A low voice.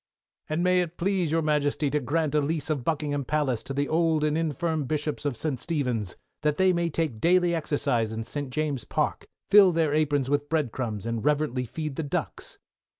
No: medium, 150 Hz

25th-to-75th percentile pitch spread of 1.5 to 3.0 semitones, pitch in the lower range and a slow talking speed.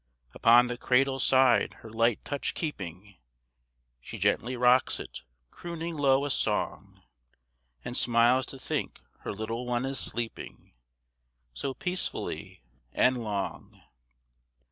Yes: narrow, 2.6 semitones; low, 125 Hz; slow, 120 wpm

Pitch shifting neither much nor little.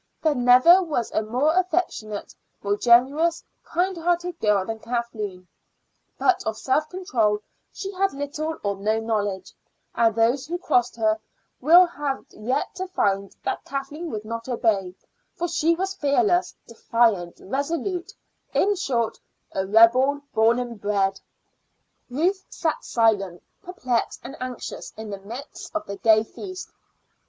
No: wide, 7.5 semitones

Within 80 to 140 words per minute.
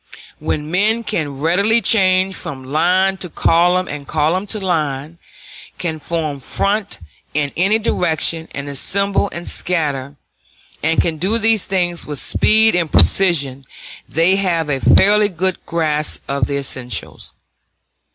Yes: slow, 135 wpm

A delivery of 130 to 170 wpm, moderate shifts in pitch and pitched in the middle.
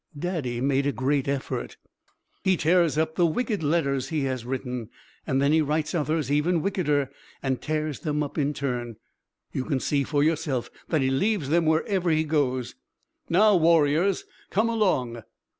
Yes: average, 160 wpm; average, 3.7 semitones; medium, 150 Hz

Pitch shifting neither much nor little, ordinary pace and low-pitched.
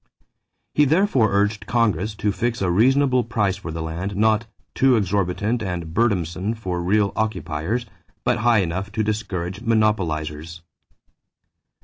No: average, 4.2 semitones; slow, 130 wpm; low, 105 Hz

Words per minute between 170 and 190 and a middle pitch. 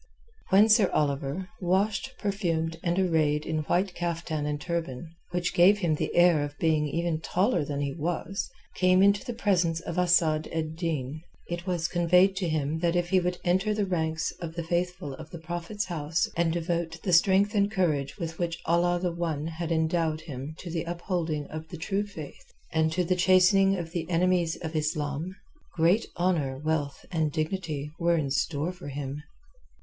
Yes: average, 185 wpm; medium, 170 Hz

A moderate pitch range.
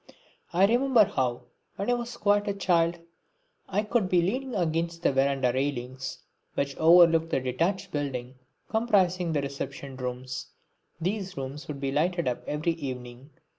No: wide, 6.1 semitones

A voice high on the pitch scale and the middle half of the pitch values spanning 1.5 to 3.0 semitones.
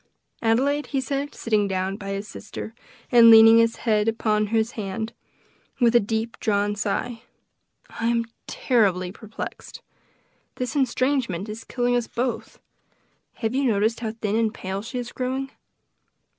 Yes: high, 225 Hz; narrow, 2.6 semitones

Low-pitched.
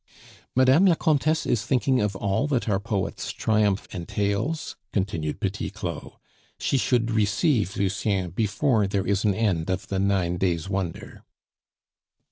Yes: low, 100 Hz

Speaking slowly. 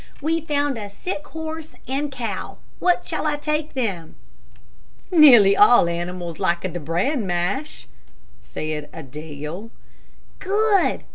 Yes: slow, 120 wpm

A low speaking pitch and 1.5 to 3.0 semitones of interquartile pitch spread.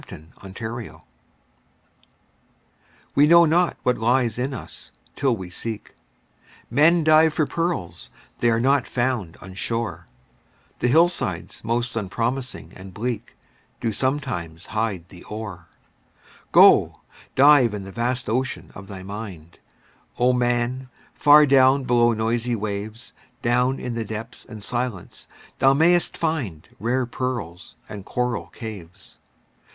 No: low, 120 Hz; average, 4.3 semitones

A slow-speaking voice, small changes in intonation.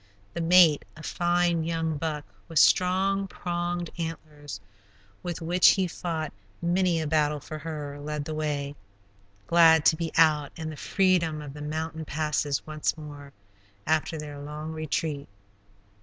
No: average, 145 wpm; narrow, 2.2 semitones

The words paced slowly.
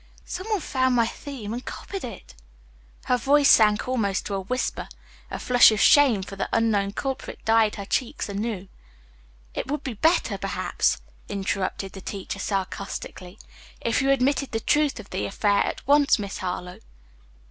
No: average, 165 wpm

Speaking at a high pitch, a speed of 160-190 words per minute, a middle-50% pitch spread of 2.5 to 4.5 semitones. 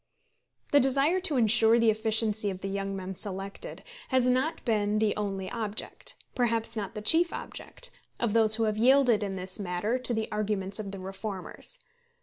Yes: high, 215 Hz; average, 175 wpm; average, 3.5 semitones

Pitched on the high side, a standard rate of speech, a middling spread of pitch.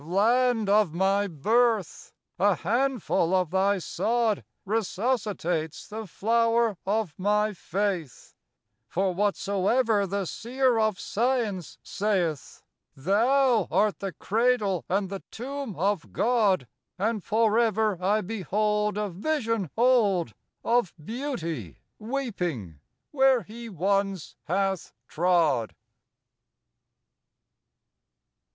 No: high, 205 Hz; slow, 95 wpm; average, 3.8 semitones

